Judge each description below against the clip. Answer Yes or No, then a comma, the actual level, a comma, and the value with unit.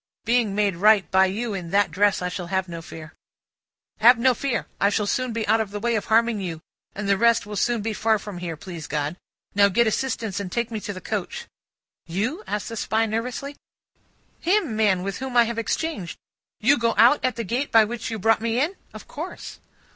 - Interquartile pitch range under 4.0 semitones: Yes, average, 3.3 semitones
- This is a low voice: No, high, 220 Hz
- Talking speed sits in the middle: No, fast, 220 wpm